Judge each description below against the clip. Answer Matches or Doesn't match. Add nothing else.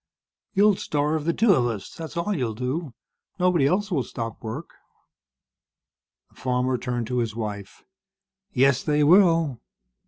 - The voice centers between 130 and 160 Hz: Matches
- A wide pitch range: Matches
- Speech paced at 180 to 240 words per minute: Doesn't match